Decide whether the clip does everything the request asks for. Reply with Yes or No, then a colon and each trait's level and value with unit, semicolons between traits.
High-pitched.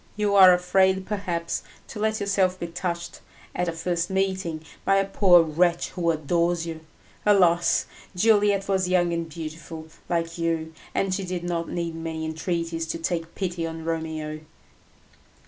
No: medium, 170 Hz